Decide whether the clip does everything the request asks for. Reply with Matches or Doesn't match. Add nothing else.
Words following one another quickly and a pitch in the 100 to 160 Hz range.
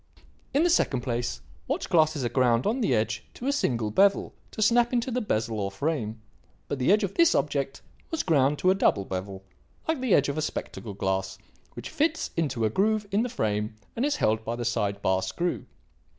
Matches